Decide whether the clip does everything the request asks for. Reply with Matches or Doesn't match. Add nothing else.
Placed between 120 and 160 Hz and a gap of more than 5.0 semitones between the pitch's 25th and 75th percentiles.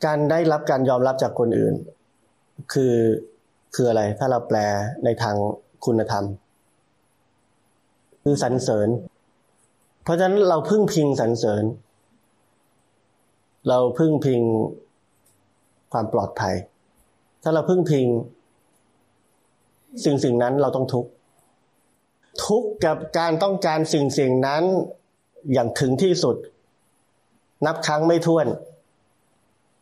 Matches